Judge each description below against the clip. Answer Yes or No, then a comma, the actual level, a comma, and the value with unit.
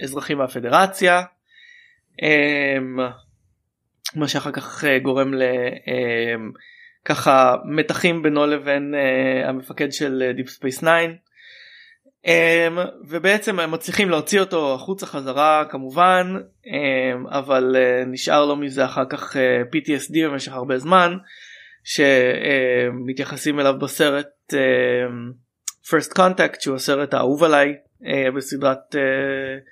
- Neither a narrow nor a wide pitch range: Yes, average, 4.2 semitones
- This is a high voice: No, medium, 140 Hz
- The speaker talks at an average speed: No, slow, 85 wpm